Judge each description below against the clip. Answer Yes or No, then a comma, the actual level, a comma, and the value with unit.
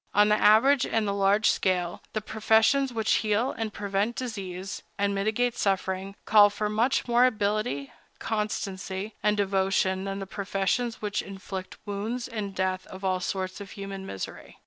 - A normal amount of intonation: No, narrow, 2.2 semitones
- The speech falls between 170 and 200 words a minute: No, average, 160 wpm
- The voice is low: No, high, 205 Hz